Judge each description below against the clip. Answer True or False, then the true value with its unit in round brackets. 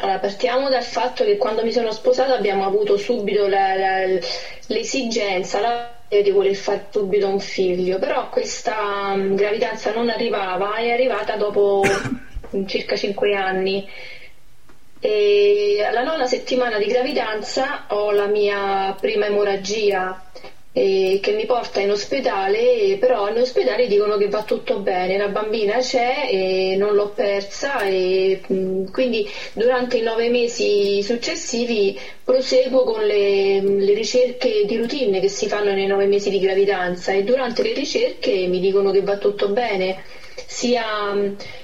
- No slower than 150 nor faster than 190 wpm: False (140 wpm)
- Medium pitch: False (210 Hz)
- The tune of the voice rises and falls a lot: False (4.7 semitones)